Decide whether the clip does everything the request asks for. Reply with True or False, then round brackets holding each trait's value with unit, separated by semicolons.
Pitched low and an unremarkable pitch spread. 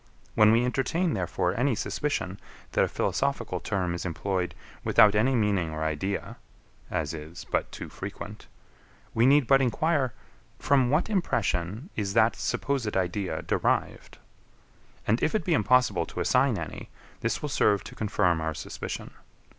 False (105 Hz; 6.7 semitones)